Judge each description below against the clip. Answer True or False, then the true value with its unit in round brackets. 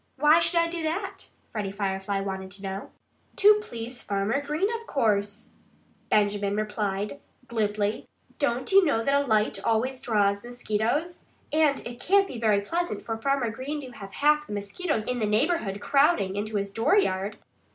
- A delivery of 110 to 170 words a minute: True (165 wpm)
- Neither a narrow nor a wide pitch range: False (6.5 semitones)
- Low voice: False (225 Hz)